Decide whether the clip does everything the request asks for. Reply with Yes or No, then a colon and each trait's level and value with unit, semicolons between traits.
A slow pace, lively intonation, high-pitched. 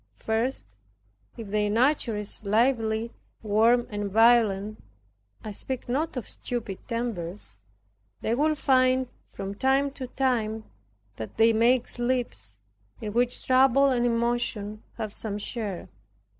No: slow, 125 wpm; average, 3.2 semitones; high, 230 Hz